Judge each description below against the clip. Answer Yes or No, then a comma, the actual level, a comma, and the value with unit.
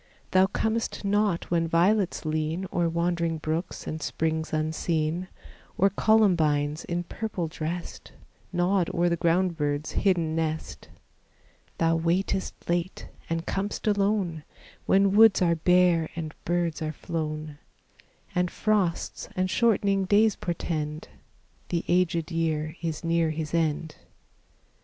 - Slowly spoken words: Yes, slow, 125 wpm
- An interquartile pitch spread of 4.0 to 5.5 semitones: No, average, 2.8 semitones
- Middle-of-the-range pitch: Yes, medium, 170 Hz